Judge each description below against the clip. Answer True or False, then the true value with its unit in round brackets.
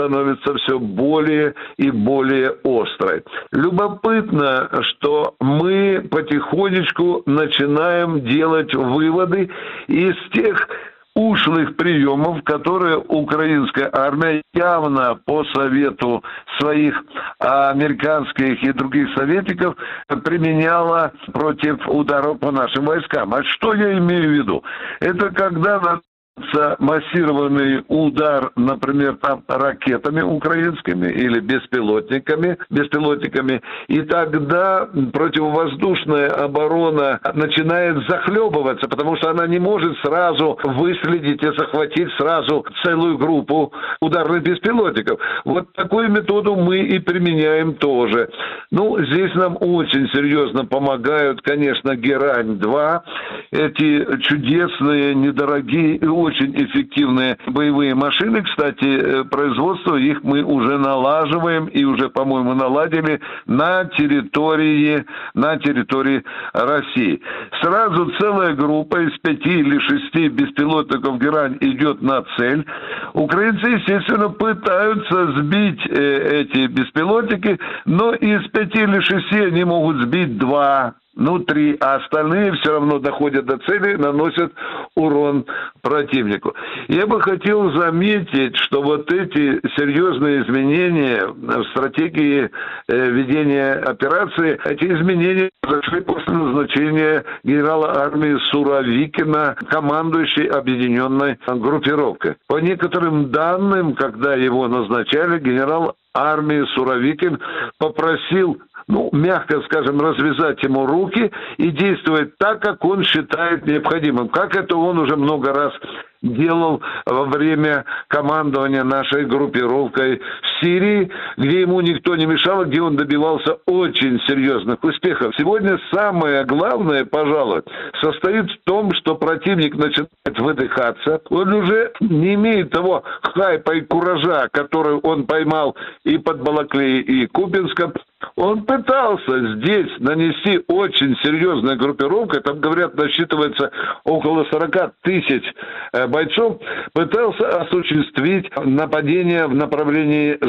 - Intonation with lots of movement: False (4.0 semitones)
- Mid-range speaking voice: True (155 Hz)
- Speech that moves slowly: True (105 wpm)